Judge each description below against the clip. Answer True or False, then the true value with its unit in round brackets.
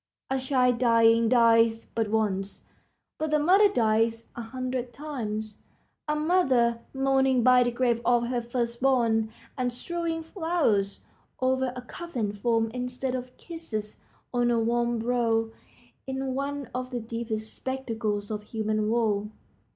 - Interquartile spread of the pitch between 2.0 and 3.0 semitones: True (2.6 semitones)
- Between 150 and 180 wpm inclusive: False (140 wpm)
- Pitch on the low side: False (240 Hz)